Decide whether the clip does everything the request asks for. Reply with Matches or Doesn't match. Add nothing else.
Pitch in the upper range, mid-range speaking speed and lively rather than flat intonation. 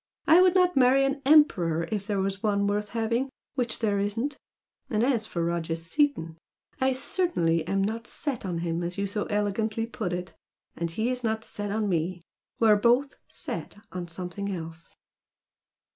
Matches